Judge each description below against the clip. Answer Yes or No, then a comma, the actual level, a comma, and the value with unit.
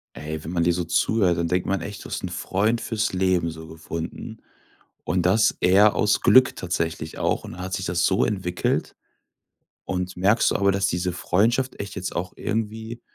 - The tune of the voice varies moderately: Yes, average, 3.1 semitones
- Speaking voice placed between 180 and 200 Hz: No, very low, 90 Hz